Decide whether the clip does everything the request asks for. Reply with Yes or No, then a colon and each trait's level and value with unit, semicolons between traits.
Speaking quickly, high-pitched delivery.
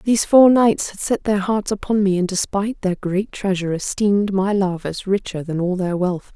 Yes: fast, 215 wpm; high, 195 Hz